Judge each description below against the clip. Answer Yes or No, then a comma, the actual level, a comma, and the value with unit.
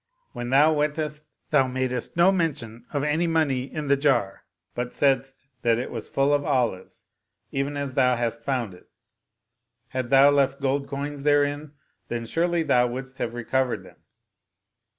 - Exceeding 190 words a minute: No, average, 160 wpm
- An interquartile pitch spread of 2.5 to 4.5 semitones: Yes, average, 2.9 semitones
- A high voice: No, low, 135 Hz